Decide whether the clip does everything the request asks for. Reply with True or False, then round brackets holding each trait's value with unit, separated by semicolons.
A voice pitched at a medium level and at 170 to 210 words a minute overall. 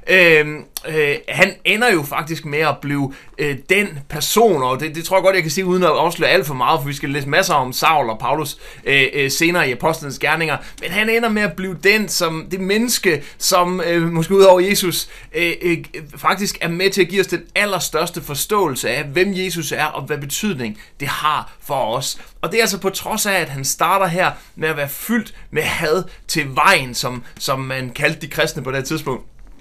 False (165 Hz; 220 wpm)